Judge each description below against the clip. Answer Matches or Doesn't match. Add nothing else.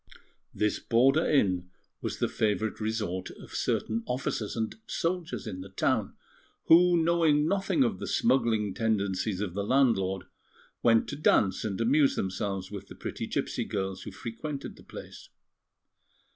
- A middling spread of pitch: Doesn't match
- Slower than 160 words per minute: Matches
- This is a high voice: Doesn't match